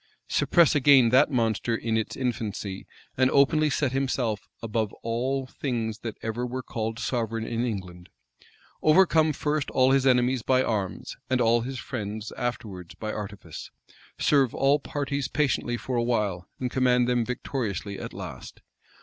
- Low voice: Yes, low, 120 Hz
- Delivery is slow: No, average, 155 wpm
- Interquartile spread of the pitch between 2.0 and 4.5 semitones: Yes, average, 3.2 semitones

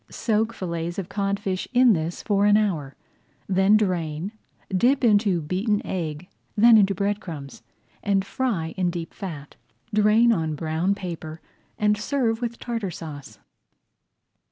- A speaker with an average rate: No, slow, 130 wpm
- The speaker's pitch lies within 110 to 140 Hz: No, high, 195 Hz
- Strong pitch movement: No, average, 4.3 semitones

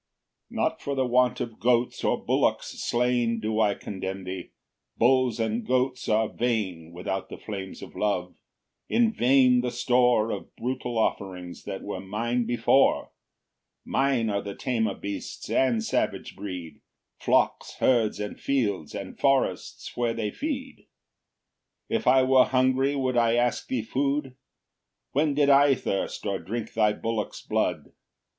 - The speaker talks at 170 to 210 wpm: No, average, 150 wpm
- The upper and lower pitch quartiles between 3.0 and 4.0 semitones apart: Yes, average, 3.7 semitones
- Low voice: Yes, low, 120 Hz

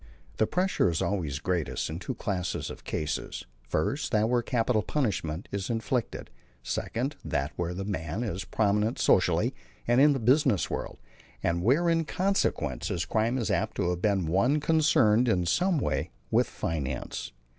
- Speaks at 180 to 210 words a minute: No, average, 165 wpm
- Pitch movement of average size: No, wide, 6.6 semitones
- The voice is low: Yes, low, 105 Hz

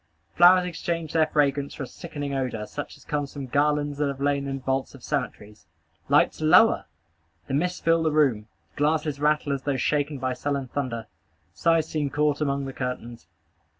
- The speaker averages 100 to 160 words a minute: No, average, 175 wpm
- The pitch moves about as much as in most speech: No, narrow, 2.2 semitones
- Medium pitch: Yes, medium, 145 Hz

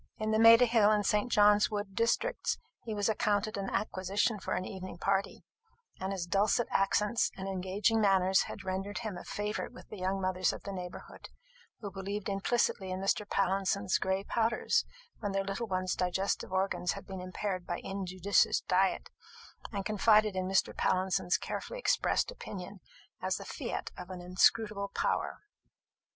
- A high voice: Yes, high, 195 Hz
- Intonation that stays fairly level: Yes, narrow, 2.0 semitones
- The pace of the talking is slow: No, average, 165 wpm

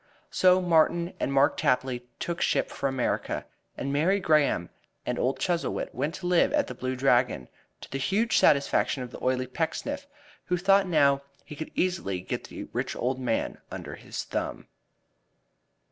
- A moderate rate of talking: Yes, average, 165 wpm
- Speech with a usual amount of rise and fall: No, wide, 5.7 semitones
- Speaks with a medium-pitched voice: Yes, medium, 145 Hz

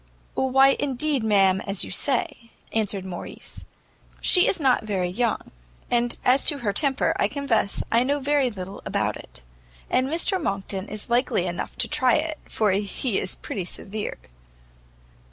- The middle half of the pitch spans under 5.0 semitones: No, wide, 5.6 semitones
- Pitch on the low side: No, high, 235 Hz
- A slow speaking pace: No, average, 155 wpm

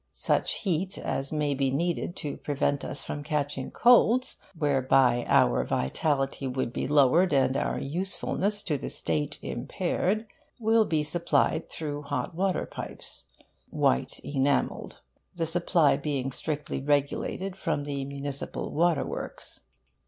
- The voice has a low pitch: No, medium, 145 Hz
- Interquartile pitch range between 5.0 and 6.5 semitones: No, average, 4.0 semitones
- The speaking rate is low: Yes, slow, 130 wpm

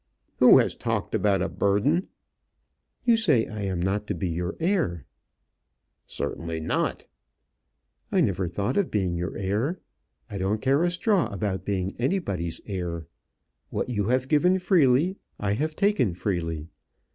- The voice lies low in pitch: Yes, low, 105 Hz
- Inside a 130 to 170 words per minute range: Yes, average, 145 wpm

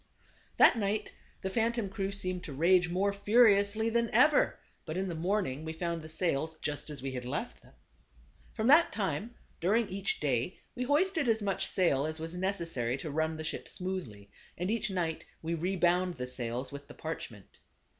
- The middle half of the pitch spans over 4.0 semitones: Yes, average, 4.5 semitones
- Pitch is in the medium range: Yes, medium, 180 Hz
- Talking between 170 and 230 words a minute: Yes, average, 185 wpm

